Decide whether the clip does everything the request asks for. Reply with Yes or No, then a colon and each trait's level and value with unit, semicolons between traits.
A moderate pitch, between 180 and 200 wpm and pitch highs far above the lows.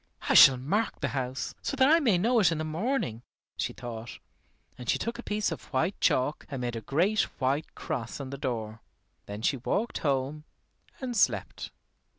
Yes: medium, 145 Hz; average, 190 wpm; wide, 8.7 semitones